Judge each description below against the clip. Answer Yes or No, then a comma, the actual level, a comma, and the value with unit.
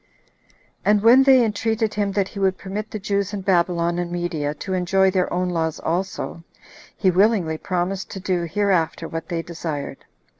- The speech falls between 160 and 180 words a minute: Yes, average, 175 wpm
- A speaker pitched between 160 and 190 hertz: Yes, medium, 185 Hz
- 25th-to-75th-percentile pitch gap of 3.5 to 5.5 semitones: No, average, 2.9 semitones